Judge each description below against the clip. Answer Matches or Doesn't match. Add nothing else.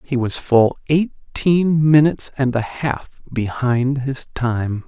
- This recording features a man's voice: Matches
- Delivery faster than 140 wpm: Doesn't match